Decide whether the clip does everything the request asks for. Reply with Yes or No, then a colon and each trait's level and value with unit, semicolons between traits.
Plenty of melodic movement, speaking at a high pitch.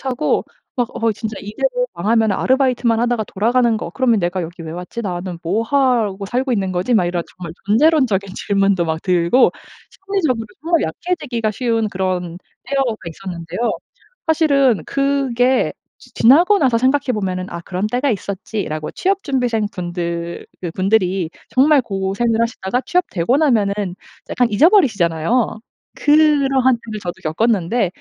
Yes: wide, 5.8 semitones; high, 225 Hz